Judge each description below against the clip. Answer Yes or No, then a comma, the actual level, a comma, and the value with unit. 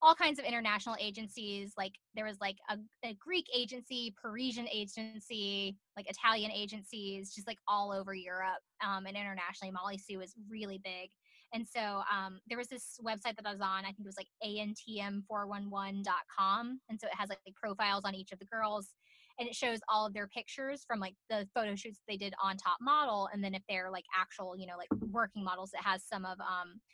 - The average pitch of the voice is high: Yes, high, 205 Hz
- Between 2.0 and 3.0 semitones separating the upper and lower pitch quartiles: Yes, narrow, 2.6 semitones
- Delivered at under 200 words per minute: No, fast, 205 wpm